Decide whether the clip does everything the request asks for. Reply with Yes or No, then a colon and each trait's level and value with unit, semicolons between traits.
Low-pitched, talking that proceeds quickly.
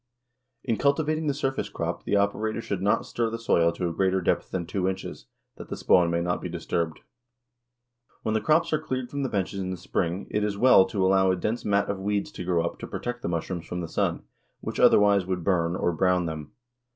Yes: very low, 95 Hz; fast, 225 wpm